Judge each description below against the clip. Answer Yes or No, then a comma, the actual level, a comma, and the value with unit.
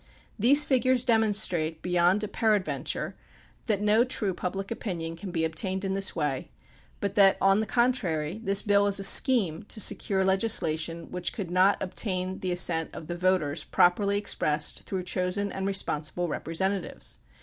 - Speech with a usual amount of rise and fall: Yes, average, 3.0 semitones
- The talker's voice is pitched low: No, high, 190 Hz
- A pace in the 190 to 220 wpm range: No, average, 160 wpm